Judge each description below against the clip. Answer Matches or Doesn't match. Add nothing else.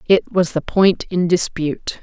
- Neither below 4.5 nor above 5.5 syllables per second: Doesn't match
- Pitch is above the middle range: Doesn't match